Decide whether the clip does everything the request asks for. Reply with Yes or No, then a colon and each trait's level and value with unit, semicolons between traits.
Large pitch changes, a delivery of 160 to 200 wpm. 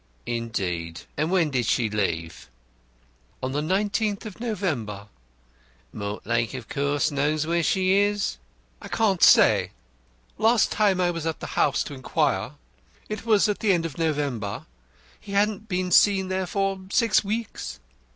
No: wide, 8.3 semitones; average, 150 wpm